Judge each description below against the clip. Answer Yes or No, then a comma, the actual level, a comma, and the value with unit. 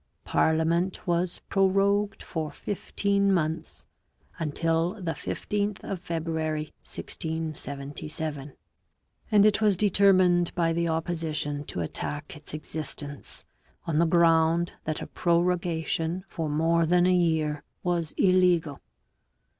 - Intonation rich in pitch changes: No, narrow, 2.5 semitones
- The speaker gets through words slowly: Yes, slow, 110 wpm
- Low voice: No, medium, 165 Hz